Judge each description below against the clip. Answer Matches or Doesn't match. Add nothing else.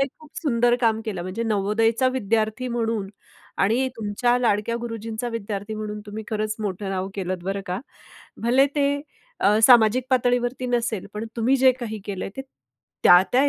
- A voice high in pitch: Matches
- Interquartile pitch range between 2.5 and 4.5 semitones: Matches